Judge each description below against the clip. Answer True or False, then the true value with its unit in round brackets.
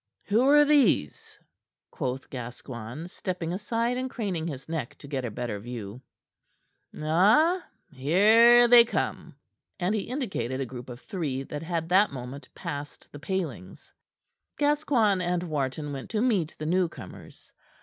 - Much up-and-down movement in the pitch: True (8.5 semitones)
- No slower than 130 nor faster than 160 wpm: True (140 wpm)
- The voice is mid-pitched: True (165 Hz)